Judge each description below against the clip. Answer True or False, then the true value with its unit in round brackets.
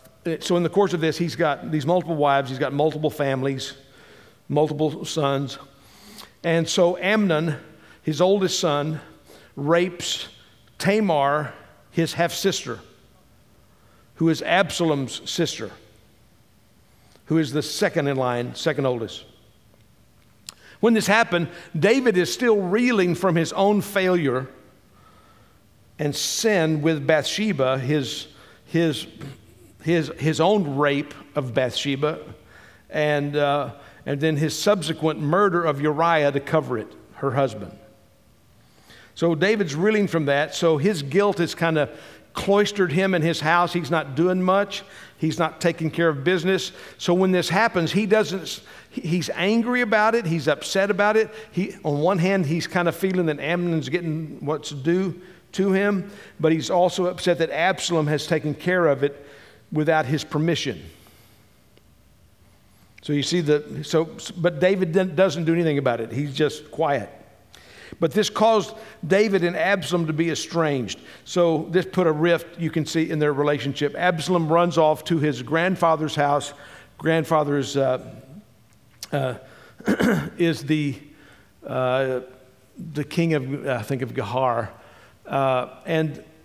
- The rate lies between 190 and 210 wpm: False (140 wpm)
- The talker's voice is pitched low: False (160 Hz)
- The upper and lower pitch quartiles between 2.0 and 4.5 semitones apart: True (4.0 semitones)